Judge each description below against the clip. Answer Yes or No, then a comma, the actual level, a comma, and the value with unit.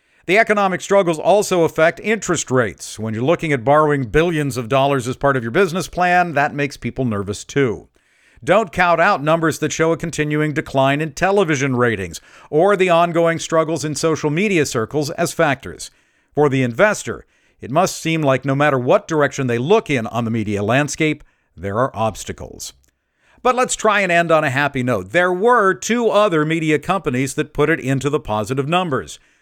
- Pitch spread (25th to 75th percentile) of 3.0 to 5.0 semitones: Yes, average, 4.6 semitones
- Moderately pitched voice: Yes, medium, 150 Hz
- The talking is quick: No, average, 185 wpm